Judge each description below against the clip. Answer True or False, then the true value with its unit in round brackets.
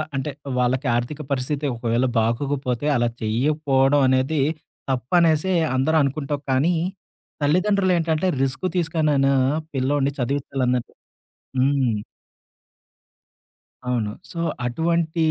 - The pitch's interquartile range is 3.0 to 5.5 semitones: True (3.5 semitones)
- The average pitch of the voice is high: False (140 Hz)